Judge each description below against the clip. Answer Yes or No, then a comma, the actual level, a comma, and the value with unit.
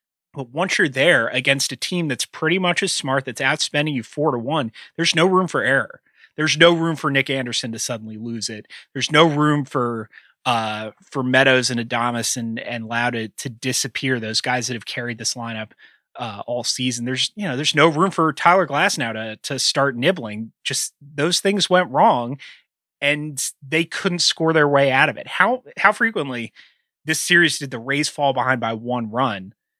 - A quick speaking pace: No, average, 195 wpm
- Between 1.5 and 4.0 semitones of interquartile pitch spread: No, average, 4.8 semitones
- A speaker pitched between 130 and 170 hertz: Yes, low, 135 Hz